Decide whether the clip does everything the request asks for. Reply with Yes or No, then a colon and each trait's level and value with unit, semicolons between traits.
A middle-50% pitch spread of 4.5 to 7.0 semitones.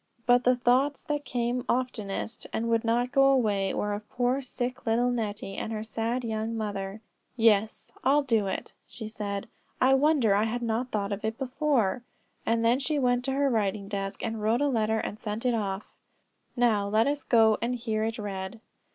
No: average, 2.8 semitones